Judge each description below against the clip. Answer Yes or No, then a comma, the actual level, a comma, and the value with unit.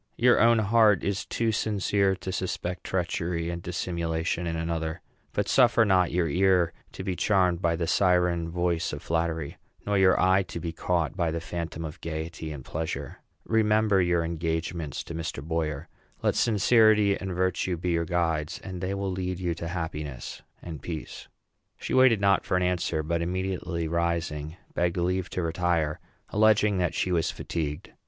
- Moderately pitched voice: No, very low, 85 Hz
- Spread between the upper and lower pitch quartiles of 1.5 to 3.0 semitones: Yes, narrow, 2.4 semitones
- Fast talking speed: No, average, 170 wpm